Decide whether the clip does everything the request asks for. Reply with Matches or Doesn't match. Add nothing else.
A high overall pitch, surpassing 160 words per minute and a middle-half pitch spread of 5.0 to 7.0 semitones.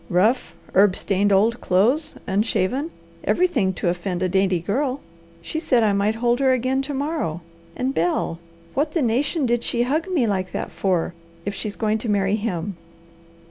Matches